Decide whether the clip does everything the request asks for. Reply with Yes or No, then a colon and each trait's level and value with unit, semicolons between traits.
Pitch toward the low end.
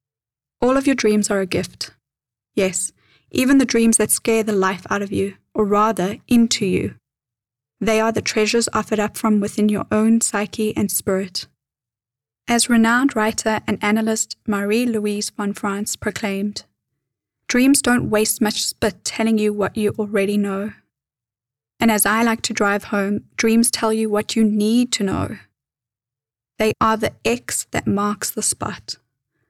No: high, 210 Hz